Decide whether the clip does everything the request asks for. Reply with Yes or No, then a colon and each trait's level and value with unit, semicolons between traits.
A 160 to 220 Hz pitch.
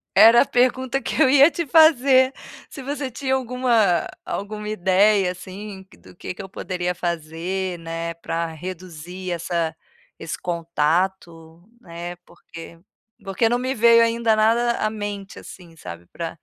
Yes: high, 190 Hz